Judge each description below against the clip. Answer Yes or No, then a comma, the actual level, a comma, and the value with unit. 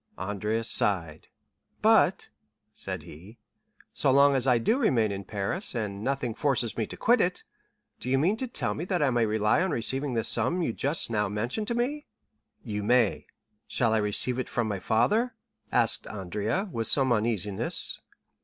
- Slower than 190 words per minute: Yes, average, 180 wpm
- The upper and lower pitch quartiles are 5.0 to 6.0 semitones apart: Yes, average, 5.3 semitones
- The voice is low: Yes, low, 120 Hz